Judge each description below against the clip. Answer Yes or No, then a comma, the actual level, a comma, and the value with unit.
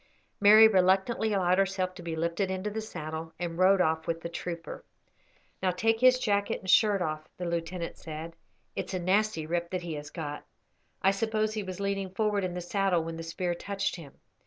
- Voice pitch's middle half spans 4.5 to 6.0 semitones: No, average, 3.1 semitones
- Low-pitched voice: No, medium, 185 Hz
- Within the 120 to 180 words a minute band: No, average, 200 wpm